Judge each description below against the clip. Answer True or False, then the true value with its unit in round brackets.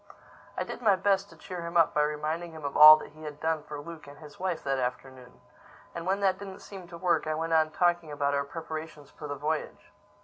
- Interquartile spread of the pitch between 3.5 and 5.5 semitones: False (2.8 semitones)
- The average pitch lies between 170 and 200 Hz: False (160 Hz)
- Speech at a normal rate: False (235 wpm)